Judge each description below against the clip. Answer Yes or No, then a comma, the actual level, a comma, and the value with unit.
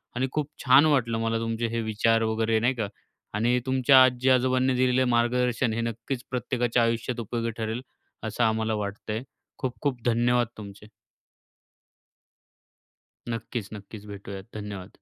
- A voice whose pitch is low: Yes, low, 115 Hz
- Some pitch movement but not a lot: No, narrow, 2.3 semitones